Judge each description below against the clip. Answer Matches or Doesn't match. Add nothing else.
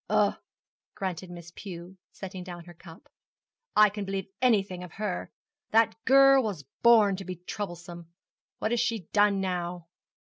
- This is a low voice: Doesn't match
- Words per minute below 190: Matches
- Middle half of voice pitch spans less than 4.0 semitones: Matches